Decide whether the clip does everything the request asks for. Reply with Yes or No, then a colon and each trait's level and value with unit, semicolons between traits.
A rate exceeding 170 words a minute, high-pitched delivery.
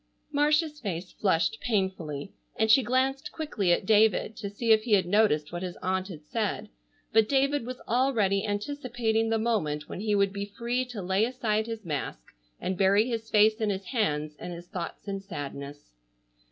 Yes: average, 180 wpm; high, 210 Hz